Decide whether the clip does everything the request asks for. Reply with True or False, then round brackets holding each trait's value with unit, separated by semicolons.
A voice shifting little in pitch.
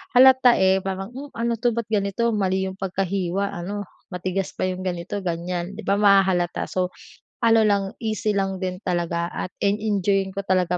True (2.1 semitones)